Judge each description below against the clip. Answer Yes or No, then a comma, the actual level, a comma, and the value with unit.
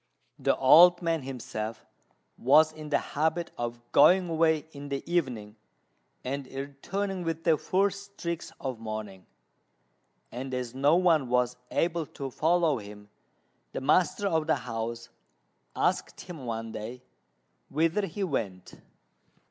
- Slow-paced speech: Yes, slow, 130 wpm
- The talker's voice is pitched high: No, medium, 145 Hz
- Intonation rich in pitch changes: Yes, wide, 5.7 semitones